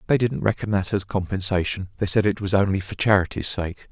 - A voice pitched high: No, low, 100 Hz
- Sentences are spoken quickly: Yes, fast, 215 wpm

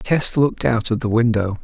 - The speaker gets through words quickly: Yes, fast, 220 wpm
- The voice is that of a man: Yes, male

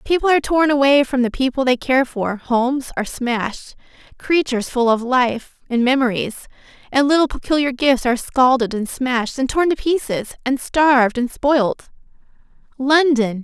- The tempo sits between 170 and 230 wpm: No, average, 160 wpm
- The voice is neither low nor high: No, very high, 260 Hz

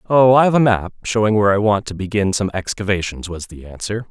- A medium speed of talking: No, fast, 235 wpm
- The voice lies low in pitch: Yes, low, 105 Hz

